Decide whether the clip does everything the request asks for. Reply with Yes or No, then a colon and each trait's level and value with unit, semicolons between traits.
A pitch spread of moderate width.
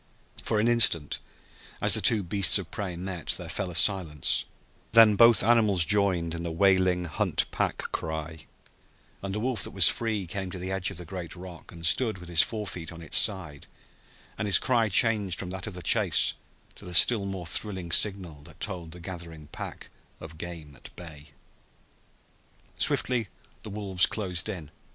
Yes: average, 3.5 semitones